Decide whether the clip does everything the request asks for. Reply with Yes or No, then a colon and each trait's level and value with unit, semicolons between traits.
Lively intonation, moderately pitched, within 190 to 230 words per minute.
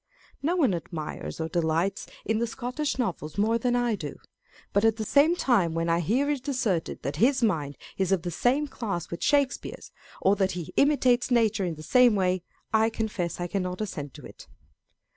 No: wide, 6.2 semitones; high, 210 Hz; average, 195 wpm